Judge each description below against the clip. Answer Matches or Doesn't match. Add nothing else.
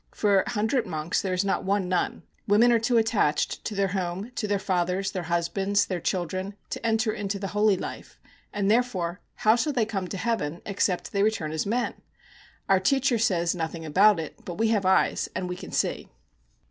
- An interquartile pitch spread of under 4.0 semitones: Matches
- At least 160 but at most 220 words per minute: Matches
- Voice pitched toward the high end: Matches